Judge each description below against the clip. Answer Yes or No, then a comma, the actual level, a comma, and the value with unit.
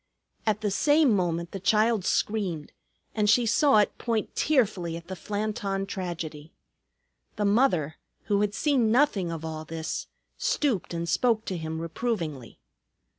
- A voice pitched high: Yes, high, 200 Hz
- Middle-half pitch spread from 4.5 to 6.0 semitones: Yes, average, 4.9 semitones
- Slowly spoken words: No, average, 145 wpm